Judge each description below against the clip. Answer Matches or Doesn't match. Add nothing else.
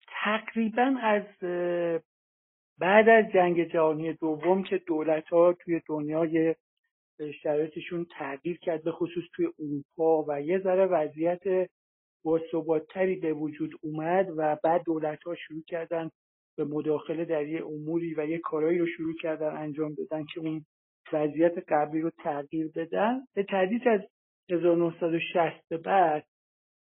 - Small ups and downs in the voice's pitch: Matches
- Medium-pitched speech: Matches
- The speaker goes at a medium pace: Matches